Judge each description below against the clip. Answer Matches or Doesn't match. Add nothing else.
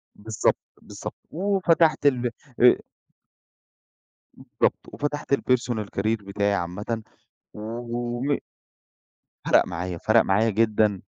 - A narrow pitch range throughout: Doesn't match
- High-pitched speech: Doesn't match